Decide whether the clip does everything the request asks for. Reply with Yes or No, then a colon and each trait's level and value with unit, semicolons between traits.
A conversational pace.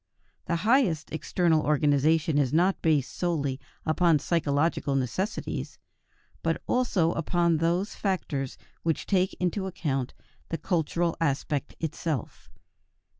No: slow, 110 wpm